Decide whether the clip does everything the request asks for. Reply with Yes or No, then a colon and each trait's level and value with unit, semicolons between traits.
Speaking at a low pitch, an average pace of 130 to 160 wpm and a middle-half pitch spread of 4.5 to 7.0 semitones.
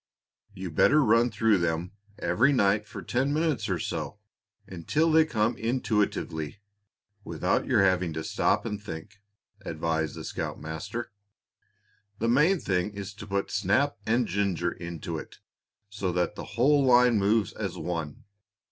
Yes: low, 105 Hz; average, 145 wpm; average, 5.3 semitones